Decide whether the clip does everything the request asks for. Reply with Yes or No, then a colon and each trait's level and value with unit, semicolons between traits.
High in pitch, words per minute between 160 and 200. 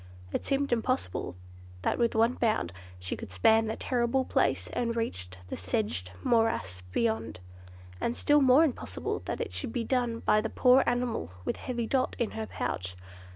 Yes: high, 225 Hz; average, 170 wpm